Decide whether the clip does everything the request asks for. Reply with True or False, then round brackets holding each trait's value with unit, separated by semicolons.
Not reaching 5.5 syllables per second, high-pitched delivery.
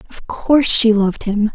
True (5.2 syllables/s; 225 Hz)